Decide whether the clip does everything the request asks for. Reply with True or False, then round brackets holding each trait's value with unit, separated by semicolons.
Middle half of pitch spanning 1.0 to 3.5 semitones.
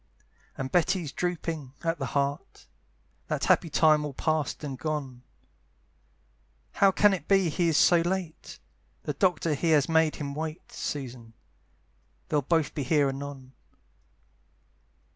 True (3.2 semitones)